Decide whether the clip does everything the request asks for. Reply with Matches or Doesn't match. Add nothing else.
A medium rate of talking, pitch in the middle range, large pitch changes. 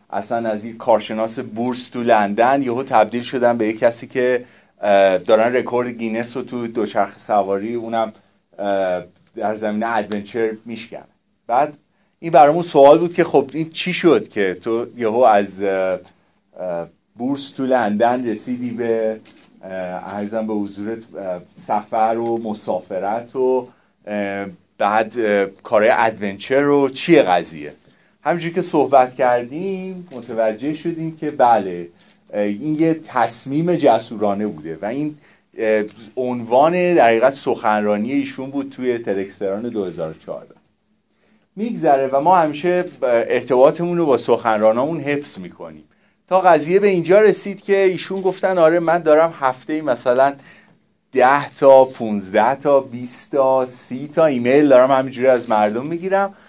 Doesn't match